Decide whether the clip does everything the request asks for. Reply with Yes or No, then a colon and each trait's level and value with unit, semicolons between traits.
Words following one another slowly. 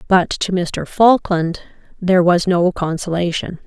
Yes: slow, 130 wpm